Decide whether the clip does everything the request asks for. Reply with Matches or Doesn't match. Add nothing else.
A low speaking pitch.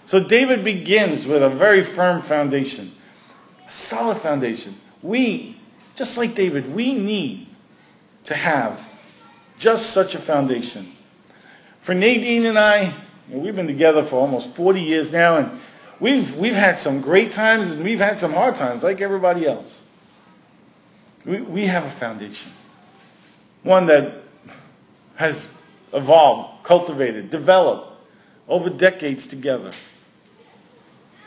Doesn't match